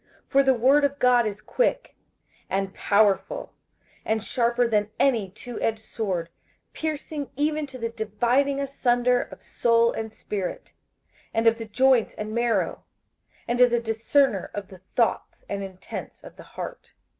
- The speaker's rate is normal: Yes, average, 155 wpm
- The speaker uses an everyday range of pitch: Yes, average, 3.6 semitones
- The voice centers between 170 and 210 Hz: No, high, 235 Hz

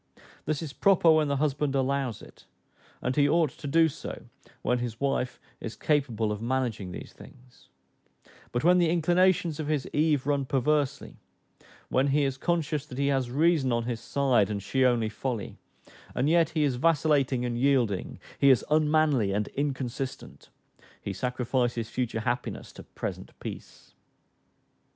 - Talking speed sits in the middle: Yes, average, 160 wpm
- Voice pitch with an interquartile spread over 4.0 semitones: No, average, 3.7 semitones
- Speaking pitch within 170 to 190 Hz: No, low, 135 Hz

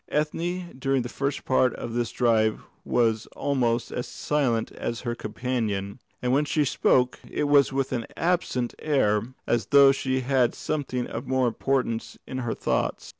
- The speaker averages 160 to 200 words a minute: Yes, average, 165 wpm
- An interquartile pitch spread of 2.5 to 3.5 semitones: Yes, average, 2.9 semitones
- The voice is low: Yes, low, 130 Hz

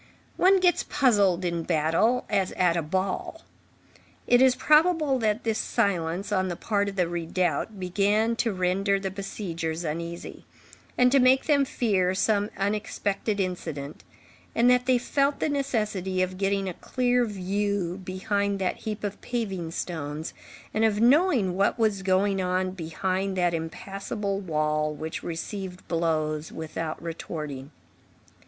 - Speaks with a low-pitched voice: No, high, 195 Hz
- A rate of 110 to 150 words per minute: Yes, average, 145 wpm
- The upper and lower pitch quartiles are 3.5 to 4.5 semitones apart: Yes, average, 4.2 semitones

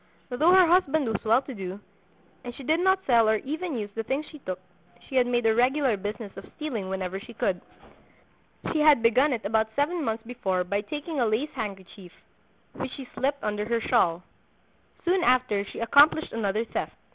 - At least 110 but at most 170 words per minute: No, average, 190 wpm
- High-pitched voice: Yes, high, 240 Hz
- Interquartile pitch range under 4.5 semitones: No, wide, 5.5 semitones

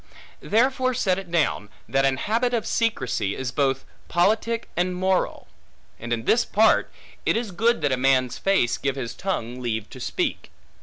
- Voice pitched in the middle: Yes, medium, 175 Hz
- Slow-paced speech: No, average, 170 wpm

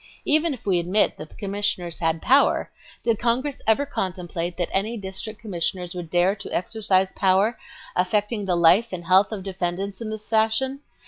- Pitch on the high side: Yes, high, 195 Hz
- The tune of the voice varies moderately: Yes, average, 3.6 semitones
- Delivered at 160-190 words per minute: Yes, average, 175 wpm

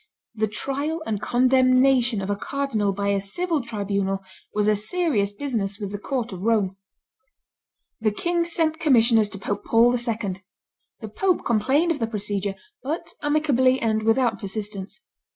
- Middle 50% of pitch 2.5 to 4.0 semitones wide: No, average, 4.9 semitones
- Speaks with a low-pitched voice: No, high, 225 Hz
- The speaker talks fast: No, average, 150 wpm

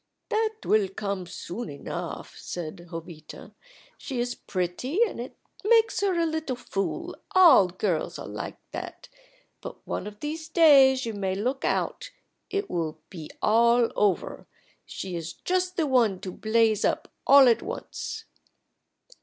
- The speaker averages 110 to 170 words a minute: Yes, average, 145 wpm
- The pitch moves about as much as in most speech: No, wide, 8.6 semitones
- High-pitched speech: Yes, high, 230 Hz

